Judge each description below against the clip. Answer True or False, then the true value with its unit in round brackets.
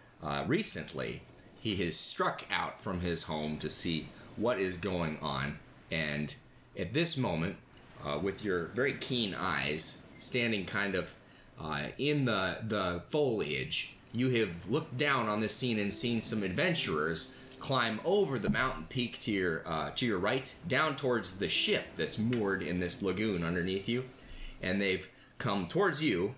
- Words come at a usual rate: True (160 wpm)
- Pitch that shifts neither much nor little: False (5.7 semitones)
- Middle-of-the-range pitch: False (105 Hz)